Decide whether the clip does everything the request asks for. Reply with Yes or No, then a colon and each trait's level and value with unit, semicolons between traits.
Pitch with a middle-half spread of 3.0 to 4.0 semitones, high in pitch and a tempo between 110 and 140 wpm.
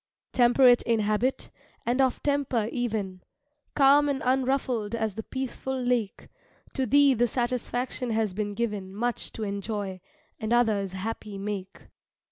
Yes: average, 3.5 semitones; high, 235 Hz; slow, 135 wpm